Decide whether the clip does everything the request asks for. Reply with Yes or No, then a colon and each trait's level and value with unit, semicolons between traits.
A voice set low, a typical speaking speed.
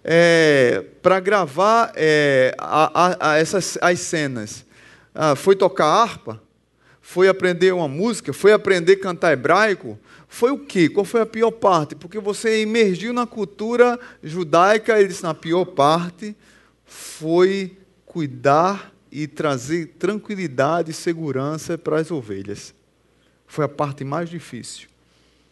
No: medium, 170 Hz; average, 130 wpm